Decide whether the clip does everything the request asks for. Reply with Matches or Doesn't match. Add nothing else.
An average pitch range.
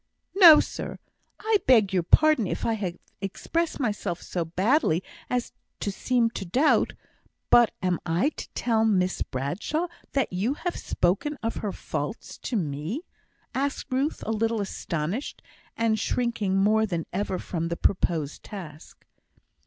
Doesn't match